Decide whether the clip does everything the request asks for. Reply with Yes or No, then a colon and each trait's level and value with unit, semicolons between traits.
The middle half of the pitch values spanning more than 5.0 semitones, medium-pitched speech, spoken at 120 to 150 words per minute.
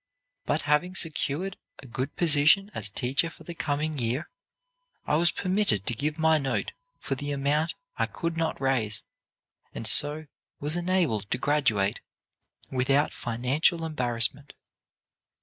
No: average, 4.3 semitones; medium, 145 Hz; slow, 135 wpm